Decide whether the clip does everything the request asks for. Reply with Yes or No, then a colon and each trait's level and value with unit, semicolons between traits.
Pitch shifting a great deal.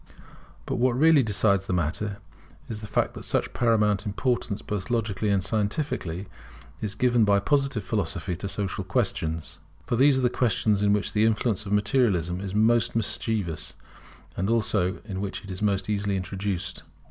No: average, 2.7 semitones